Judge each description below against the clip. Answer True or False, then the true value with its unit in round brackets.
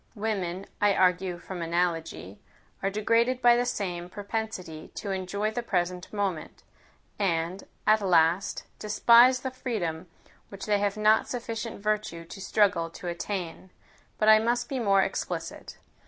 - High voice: True (200 Hz)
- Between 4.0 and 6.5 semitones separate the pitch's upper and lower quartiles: False (3.6 semitones)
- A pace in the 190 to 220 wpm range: False (140 wpm)